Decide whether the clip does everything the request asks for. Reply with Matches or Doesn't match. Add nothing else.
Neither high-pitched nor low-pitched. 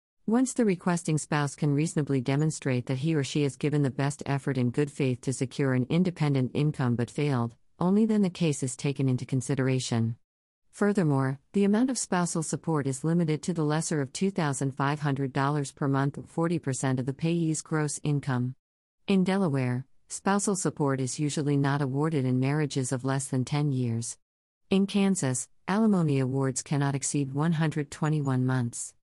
Matches